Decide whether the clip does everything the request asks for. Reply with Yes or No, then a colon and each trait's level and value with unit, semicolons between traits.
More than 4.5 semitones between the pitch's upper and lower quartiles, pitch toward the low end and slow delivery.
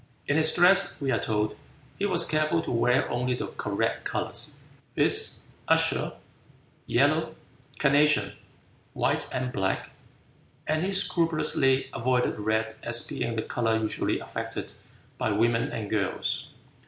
Yes: wide, 5.6 semitones; low, 130 Hz; slow, 130 wpm